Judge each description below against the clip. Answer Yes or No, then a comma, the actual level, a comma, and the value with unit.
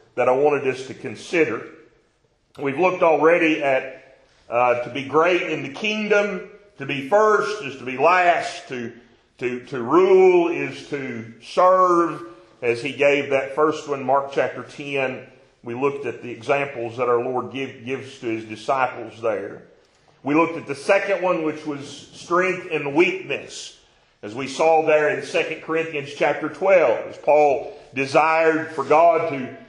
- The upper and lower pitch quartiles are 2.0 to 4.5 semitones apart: No, average, 5.2 semitones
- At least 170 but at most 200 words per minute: No, average, 160 wpm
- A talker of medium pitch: Yes, medium, 150 Hz